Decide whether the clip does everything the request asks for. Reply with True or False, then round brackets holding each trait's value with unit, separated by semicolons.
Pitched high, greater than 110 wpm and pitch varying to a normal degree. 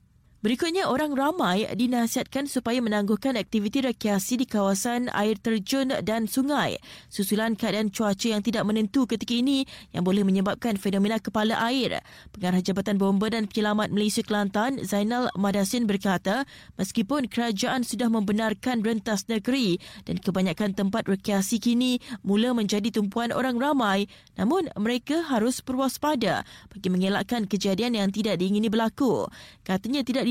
True (225 Hz; 135 wpm; 3.4 semitones)